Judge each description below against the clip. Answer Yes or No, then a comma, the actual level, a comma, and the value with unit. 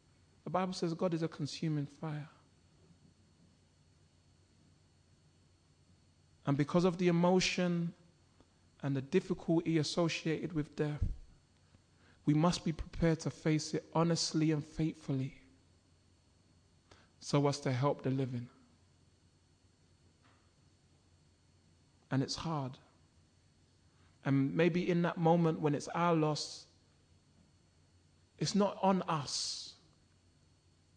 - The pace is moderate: No, slow, 100 wpm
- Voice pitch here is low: Yes, low, 120 Hz